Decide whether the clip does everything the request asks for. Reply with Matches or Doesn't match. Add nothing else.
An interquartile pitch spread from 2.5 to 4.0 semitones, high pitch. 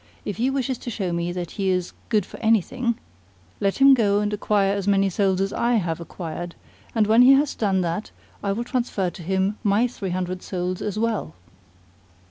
Matches